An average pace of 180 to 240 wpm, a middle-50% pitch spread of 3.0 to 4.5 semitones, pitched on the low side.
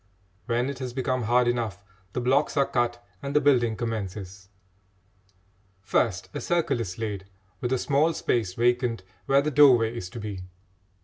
No: average, 165 wpm; average, 3.6 semitones; low, 120 Hz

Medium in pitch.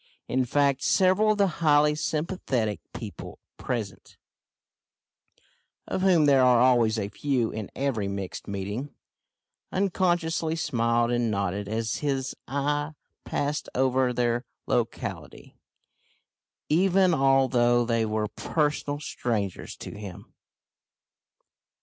No: low, 130 Hz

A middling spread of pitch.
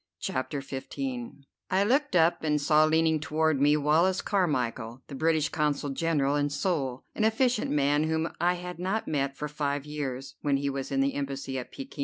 Yes: average, 3.0 semitones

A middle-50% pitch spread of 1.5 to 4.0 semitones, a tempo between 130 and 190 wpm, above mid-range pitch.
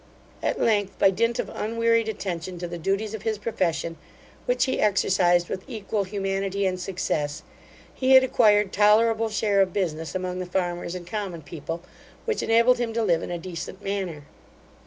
Yes: average, 3.7 semitones; average, 175 wpm; high, 195 Hz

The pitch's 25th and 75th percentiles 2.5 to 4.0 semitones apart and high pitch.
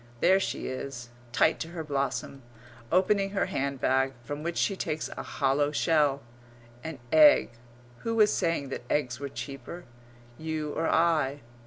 No: average, 3.7 semitones; medium, 150 Hz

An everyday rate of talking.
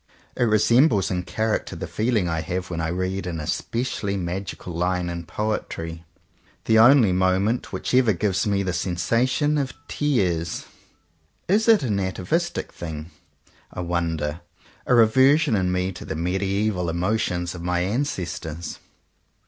Yes: average, 150 wpm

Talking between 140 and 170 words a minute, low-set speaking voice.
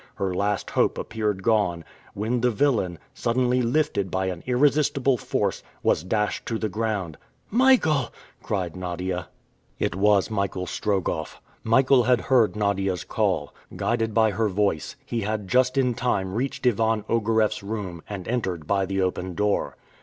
Yes: average, 150 wpm; low, 105 Hz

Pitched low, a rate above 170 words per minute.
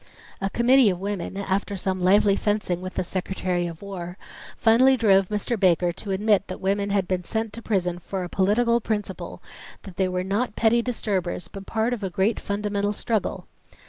No: high, 200 Hz; average, 185 wpm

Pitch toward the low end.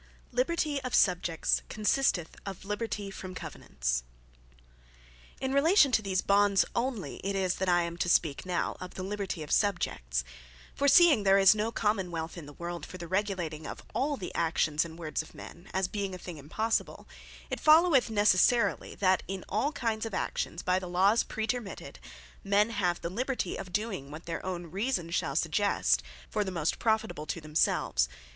No: high, 190 Hz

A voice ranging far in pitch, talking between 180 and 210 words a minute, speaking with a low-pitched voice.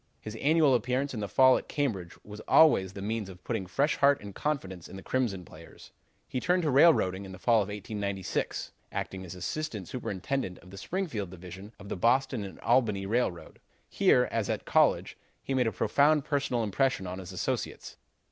Yes: wide, 6.0 semitones; average, 190 wpm; low, 110 Hz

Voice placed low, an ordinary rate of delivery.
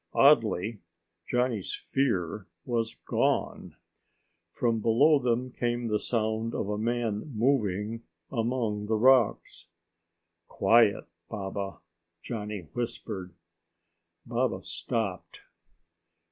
No: low, 115 Hz; slow, 90 wpm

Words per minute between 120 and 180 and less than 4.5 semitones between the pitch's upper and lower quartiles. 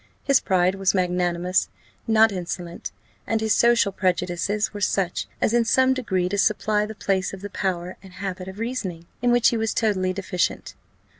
Yes: average, 175 wpm; average, 3.3 semitones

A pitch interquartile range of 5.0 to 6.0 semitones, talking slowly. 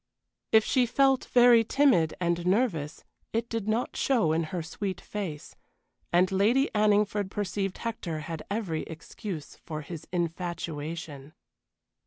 Yes: wide, 5.4 semitones; slow, 130 wpm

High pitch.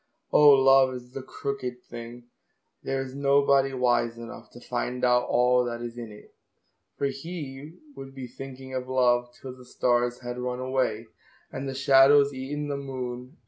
No: low, 130 Hz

